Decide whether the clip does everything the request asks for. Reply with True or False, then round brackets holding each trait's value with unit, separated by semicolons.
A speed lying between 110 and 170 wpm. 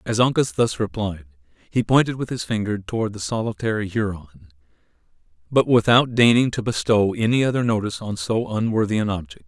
True (165 wpm)